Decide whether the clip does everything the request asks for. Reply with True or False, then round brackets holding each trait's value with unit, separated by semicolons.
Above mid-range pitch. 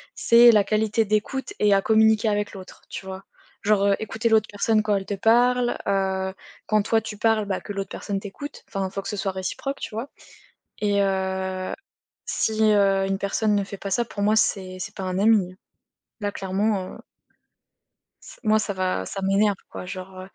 True (205 Hz)